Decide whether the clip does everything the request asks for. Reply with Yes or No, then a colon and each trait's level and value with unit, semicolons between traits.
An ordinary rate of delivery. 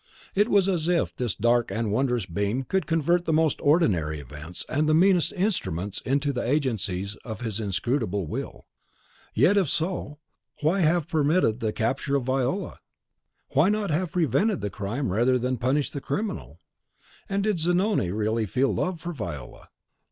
Yes: average, 165 wpm